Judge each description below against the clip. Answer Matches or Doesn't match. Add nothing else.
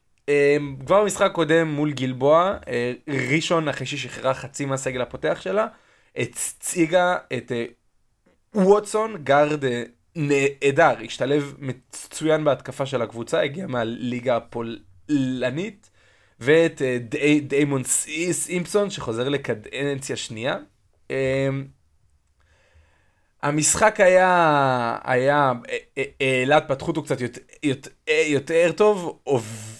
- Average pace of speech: Doesn't match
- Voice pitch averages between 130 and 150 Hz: Matches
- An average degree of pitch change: Matches